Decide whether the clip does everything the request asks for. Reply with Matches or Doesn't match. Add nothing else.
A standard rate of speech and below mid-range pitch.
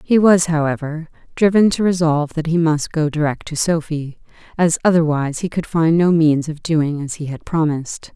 Doesn't match